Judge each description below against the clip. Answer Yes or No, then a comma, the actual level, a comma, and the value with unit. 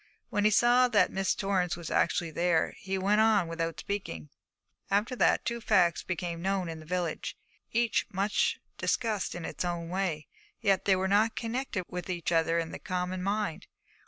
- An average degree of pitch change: Yes, average, 3.4 semitones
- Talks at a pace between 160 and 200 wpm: Yes, average, 180 wpm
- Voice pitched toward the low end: No, medium, 185 Hz